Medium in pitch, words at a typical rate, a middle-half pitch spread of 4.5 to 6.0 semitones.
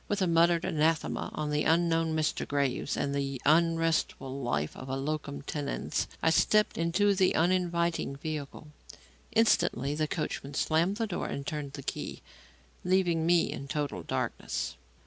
No: medium, 155 Hz; average, 150 wpm; average, 3.3 semitones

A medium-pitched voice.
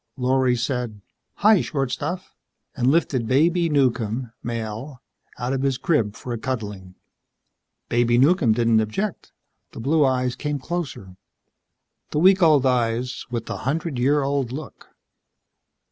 No: low, 130 Hz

